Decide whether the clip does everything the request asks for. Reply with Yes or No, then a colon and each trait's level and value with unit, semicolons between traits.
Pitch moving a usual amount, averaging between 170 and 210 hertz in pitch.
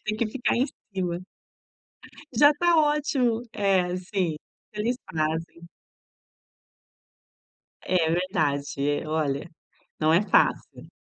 No: wide, 6.0 semitones; medium, 185 Hz